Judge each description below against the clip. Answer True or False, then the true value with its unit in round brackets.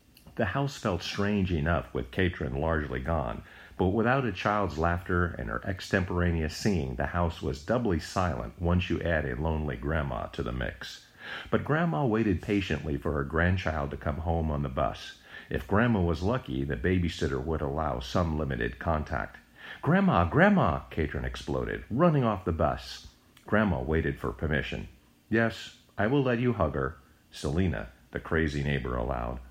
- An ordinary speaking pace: True (165 wpm)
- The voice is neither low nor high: False (80 Hz)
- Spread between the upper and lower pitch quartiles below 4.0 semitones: False (5.0 semitones)